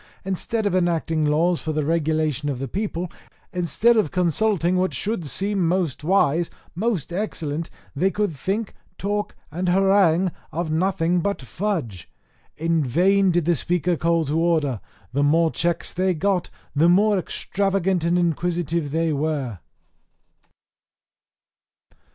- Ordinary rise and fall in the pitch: Yes, average, 3.3 semitones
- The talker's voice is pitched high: No, medium, 170 Hz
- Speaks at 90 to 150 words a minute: Yes, slow, 135 wpm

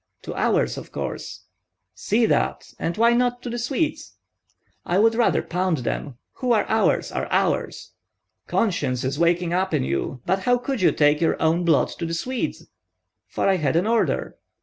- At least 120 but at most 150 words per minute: No, average, 180 wpm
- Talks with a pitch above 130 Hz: Yes, medium, 185 Hz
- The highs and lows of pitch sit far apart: Yes, wide, 6.4 semitones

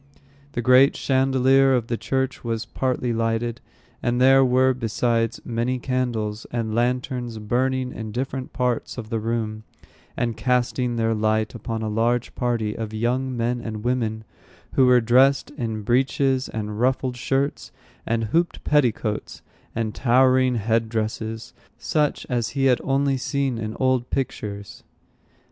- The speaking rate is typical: Yes, average, 145 wpm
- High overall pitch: No, low, 120 Hz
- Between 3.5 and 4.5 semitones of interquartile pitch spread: No, narrow, 2.5 semitones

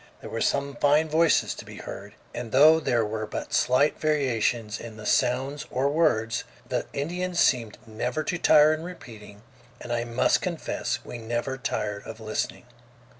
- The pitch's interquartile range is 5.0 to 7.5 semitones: Yes, average, 5.3 semitones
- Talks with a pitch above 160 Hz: No, low, 125 Hz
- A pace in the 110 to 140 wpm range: No, average, 170 wpm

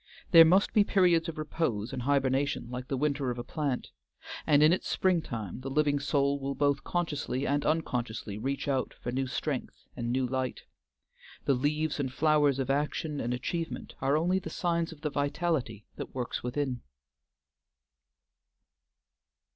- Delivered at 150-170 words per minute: Yes, average, 160 wpm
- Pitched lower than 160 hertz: Yes, medium, 140 Hz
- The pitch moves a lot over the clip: No, average, 3.4 semitones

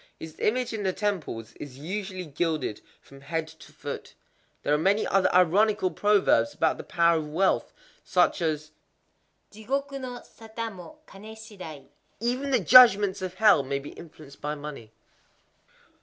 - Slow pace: No, average, 145 wpm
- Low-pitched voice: No, medium, 185 Hz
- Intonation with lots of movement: Yes, wide, 5.9 semitones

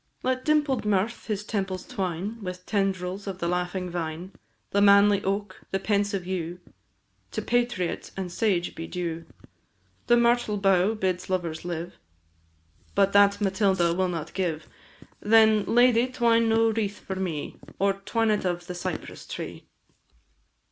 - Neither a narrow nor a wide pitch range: Yes, average, 3.1 semitones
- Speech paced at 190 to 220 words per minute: No, average, 150 wpm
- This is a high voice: Yes, high, 195 Hz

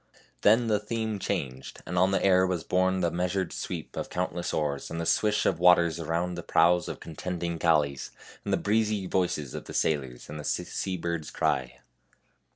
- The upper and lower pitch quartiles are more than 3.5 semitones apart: No, narrow, 2.6 semitones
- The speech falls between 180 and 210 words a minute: Yes, average, 190 wpm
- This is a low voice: Yes, very low, 90 Hz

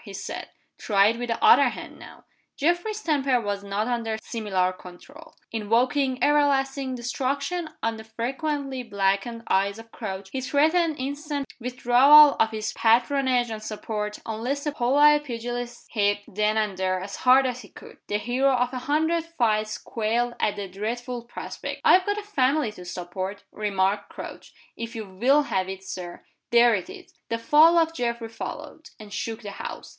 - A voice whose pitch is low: No, high, 240 Hz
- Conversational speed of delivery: Yes, average, 170 wpm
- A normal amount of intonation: Yes, average, 4.8 semitones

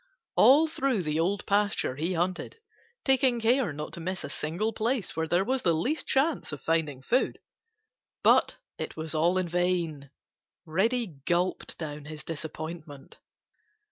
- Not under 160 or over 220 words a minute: No, average, 150 wpm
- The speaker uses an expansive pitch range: Yes, wide, 6.2 semitones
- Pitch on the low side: No, medium, 175 Hz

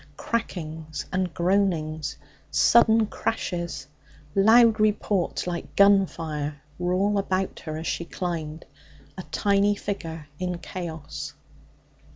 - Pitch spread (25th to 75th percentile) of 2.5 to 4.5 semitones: Yes, average, 3.9 semitones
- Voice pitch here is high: No, medium, 180 Hz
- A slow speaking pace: Yes, slow, 110 wpm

